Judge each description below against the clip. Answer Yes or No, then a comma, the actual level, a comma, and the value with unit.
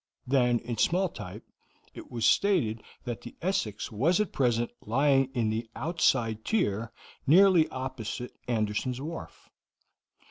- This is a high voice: No, low, 125 Hz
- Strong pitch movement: Yes, wide, 5.8 semitones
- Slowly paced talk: Yes, slow, 130 wpm